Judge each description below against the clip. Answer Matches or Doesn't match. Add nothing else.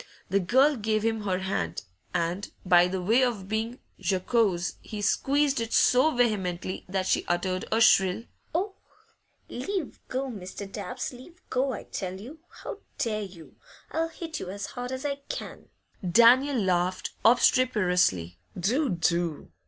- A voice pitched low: Doesn't match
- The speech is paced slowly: Doesn't match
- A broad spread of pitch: Matches